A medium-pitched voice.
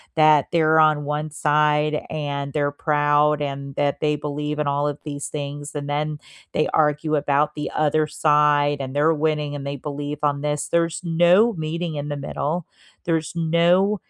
Yes: medium, 150 Hz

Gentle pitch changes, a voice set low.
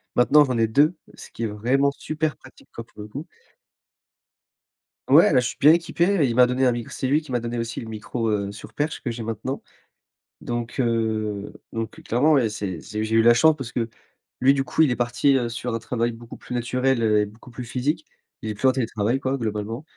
No: average, 3.0 semitones; low, 120 Hz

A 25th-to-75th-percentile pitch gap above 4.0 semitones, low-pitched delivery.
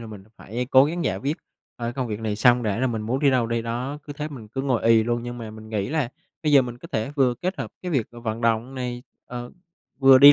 No: average, 3.0 semitones; low, 120 Hz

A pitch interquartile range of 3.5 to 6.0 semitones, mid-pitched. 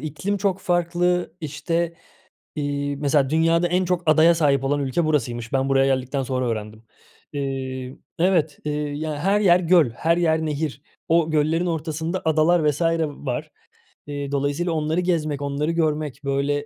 No: average, 3.1 semitones; medium, 150 Hz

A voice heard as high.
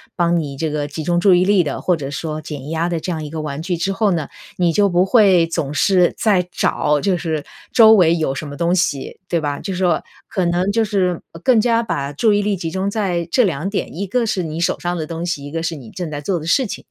No: medium, 175 Hz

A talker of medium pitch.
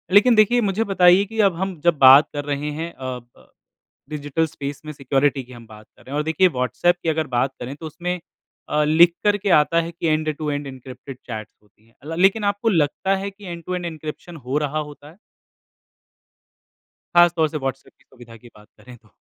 Yes: medium, 155 Hz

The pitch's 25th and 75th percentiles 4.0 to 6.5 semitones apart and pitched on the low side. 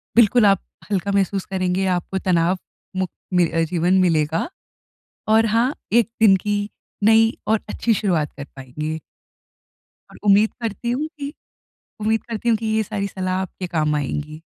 No: average, 4.4 semitones; high, 195 Hz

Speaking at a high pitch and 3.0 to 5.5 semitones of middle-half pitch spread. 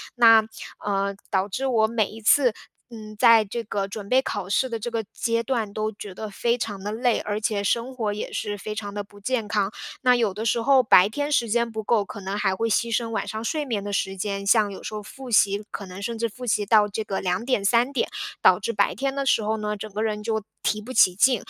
No: high, 215 Hz; narrow, 2.5 semitones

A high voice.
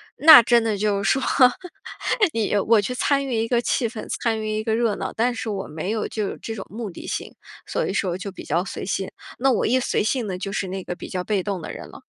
Yes: high, 215 Hz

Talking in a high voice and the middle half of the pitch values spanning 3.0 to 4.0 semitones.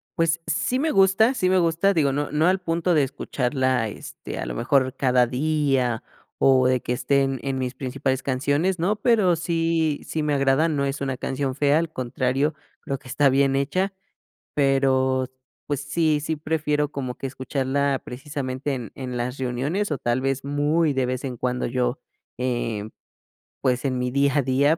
No: medium, 140 Hz; average, 3.3 semitones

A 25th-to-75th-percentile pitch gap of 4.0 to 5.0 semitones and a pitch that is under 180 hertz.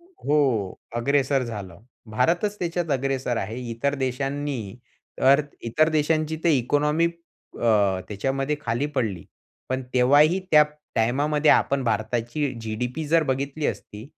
Yes: average, 4.5 semitones; low, 135 Hz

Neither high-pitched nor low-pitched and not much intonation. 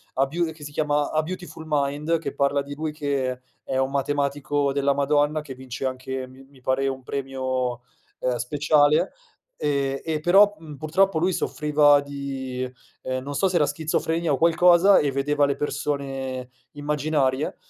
Yes: medium, 145 Hz; narrow, 2.2 semitones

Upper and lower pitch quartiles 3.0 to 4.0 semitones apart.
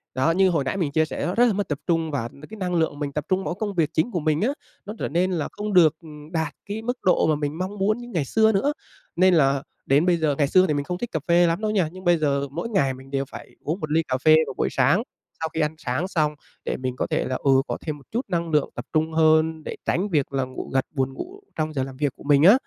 No: average, 4.5 semitones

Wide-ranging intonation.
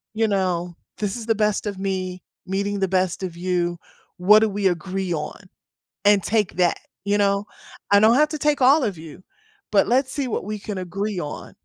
No: average, 2.7 semitones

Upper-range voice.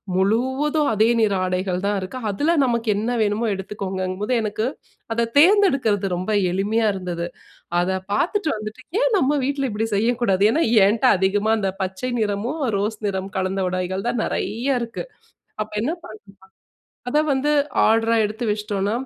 Yes: high, 215 Hz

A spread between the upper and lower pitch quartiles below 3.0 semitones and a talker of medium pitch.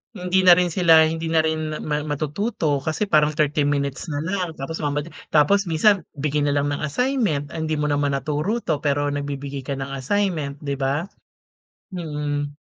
Yes: narrow, 2.4 semitones; medium, 150 Hz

